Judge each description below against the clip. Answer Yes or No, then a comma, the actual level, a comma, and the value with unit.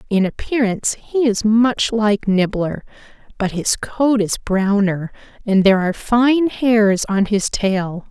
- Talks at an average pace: Yes, average, 150 wpm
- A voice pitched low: No, high, 215 Hz